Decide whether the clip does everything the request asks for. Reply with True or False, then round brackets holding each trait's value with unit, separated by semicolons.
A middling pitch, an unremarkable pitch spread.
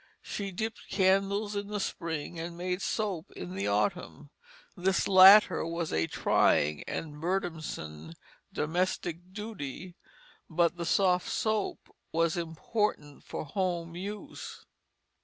True (175 Hz; 3.5 semitones)